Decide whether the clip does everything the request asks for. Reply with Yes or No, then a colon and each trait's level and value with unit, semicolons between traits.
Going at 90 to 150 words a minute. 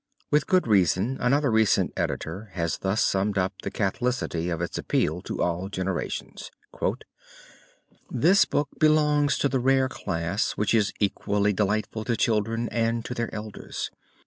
Yes: average, 145 wpm